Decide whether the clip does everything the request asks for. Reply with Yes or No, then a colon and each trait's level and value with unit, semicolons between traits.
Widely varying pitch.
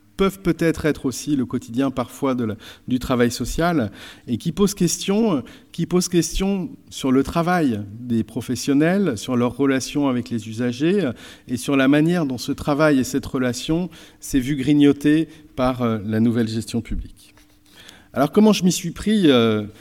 Yes: wide, 5.7 semitones